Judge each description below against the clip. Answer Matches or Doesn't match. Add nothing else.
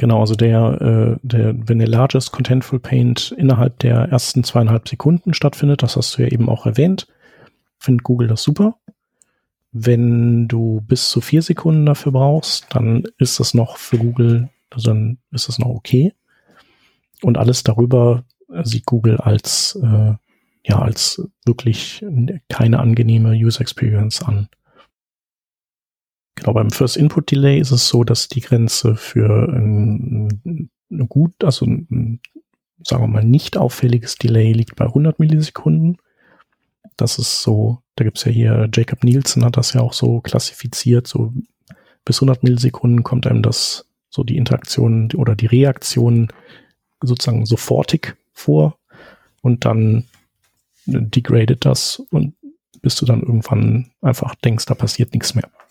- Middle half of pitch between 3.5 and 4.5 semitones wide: Doesn't match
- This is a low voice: Matches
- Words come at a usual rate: Matches